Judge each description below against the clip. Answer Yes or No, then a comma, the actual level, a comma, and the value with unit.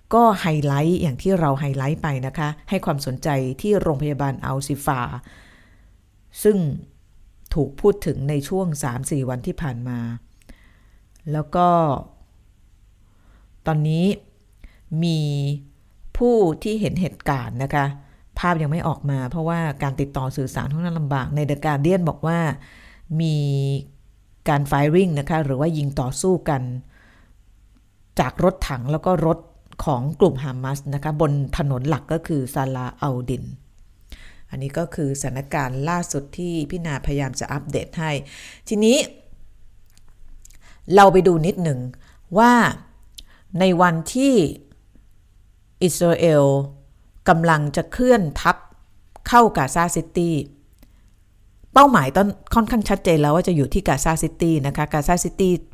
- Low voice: No, medium, 145 Hz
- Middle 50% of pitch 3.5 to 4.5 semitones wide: No, average, 5.0 semitones